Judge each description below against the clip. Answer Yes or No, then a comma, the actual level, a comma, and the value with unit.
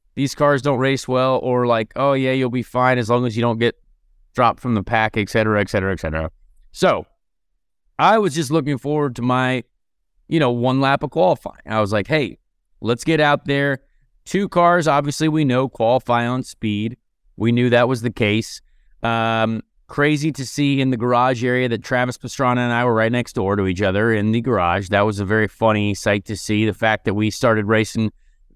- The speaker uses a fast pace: Yes, fast, 210 wpm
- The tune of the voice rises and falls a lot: No, average, 3.5 semitones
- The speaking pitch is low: Yes, low, 120 Hz